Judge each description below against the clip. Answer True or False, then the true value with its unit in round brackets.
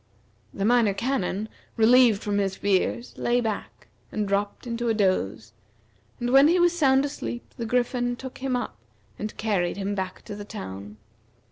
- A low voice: False (220 Hz)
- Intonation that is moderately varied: True (3.8 semitones)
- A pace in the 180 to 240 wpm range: False (165 wpm)